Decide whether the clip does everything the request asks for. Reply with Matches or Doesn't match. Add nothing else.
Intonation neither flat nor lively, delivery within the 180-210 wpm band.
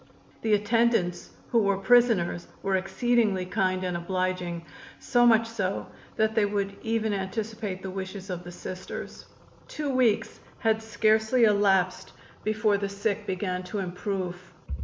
Doesn't match